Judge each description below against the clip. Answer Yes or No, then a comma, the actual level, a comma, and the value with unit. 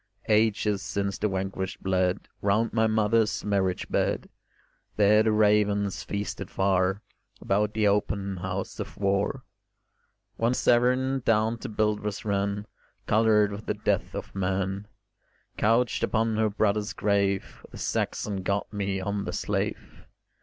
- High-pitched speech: No, low, 105 Hz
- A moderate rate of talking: No, slow, 130 wpm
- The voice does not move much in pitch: Yes, narrow, 1.7 semitones